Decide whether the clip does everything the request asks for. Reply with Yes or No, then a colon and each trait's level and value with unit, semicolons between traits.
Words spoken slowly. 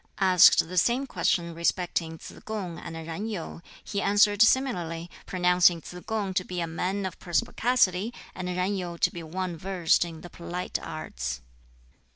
No: average, 165 wpm